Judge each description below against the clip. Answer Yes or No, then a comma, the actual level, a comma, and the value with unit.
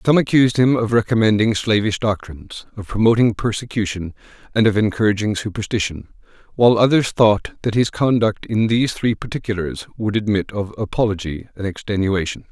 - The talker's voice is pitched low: Yes, low, 105 Hz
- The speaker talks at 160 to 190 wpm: No, average, 145 wpm